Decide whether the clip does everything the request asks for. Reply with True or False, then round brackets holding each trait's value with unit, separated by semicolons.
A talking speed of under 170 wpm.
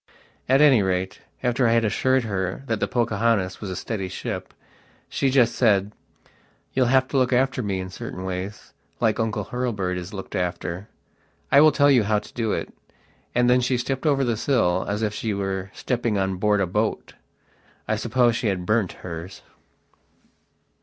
False (180 wpm)